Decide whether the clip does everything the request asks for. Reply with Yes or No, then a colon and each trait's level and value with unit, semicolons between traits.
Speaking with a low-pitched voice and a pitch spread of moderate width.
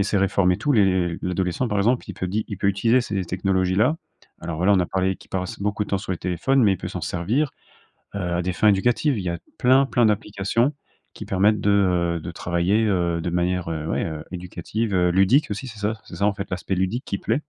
Yes: very low, 95 Hz; average, 3.1 semitones